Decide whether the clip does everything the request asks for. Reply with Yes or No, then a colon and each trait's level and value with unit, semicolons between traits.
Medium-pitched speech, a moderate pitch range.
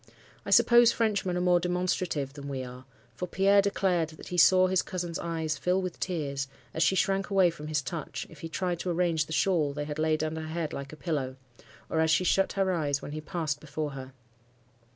Yes: medium, 165 Hz; average, 3.5 semitones